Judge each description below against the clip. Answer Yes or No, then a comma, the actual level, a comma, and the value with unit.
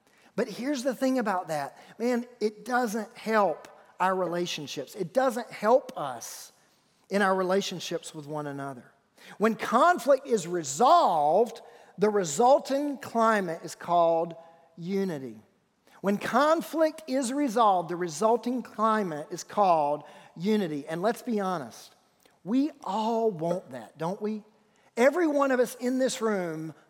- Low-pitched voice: No, high, 210 Hz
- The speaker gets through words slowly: Yes, slow, 130 wpm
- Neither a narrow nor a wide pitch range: No, wide, 6.1 semitones